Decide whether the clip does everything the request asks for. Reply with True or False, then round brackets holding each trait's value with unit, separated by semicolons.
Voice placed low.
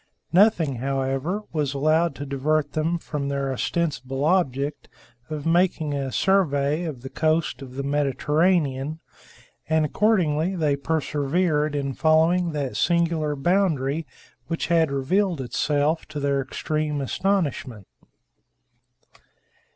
False (150 Hz)